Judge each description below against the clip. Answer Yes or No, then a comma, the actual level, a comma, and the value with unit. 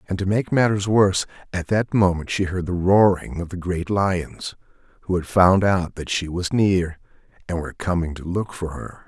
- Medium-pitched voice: No, very low, 90 Hz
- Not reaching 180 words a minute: No, fast, 205 wpm